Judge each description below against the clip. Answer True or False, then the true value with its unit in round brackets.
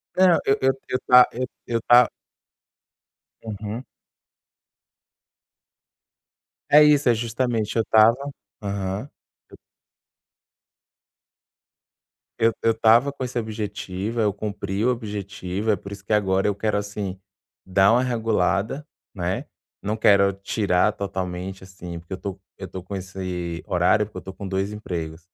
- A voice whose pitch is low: True (105 Hz)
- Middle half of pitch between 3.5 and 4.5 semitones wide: False (3.1 semitones)